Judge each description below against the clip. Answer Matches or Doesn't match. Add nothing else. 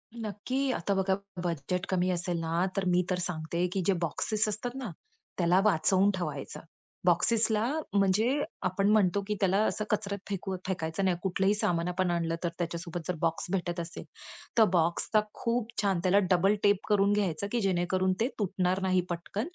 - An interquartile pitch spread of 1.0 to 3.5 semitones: Matches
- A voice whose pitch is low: Doesn't match